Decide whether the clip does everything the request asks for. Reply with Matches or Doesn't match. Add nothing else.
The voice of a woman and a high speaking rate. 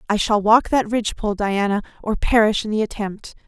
Doesn't match